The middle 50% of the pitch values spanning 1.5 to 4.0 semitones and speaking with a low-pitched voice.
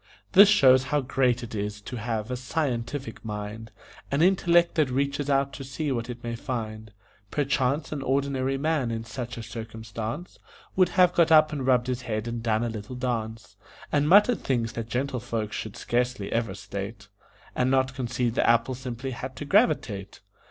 Yes: average, 3.6 semitones; low, 125 Hz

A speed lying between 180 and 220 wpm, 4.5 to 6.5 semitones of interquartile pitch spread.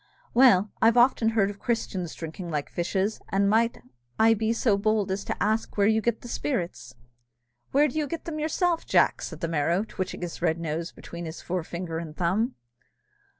Yes: average, 185 wpm; average, 5.0 semitones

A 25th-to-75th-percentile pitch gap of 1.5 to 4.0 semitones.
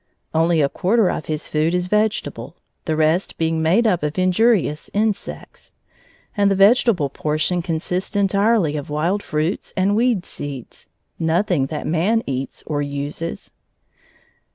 No: average, 4.6 semitones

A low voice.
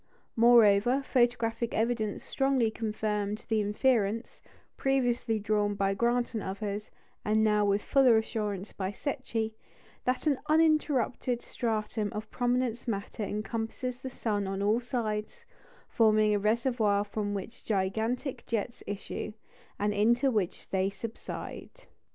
No: high, 220 Hz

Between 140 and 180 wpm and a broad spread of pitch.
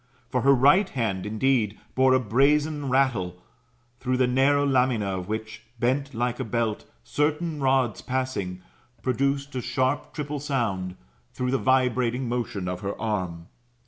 No: average, 145 wpm; average, 3.9 semitones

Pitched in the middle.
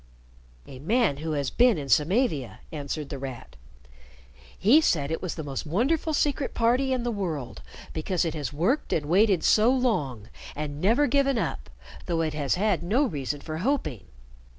Yes: medium, 170 Hz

